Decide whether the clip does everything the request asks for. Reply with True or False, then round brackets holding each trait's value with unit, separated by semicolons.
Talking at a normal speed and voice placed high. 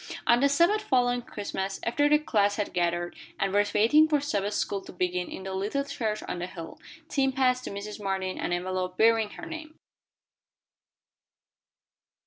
True (170 wpm; 210 Hz)